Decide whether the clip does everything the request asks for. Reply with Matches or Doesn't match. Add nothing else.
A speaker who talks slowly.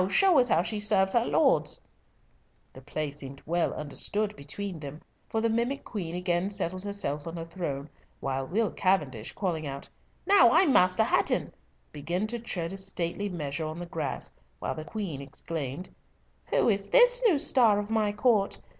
Doesn't match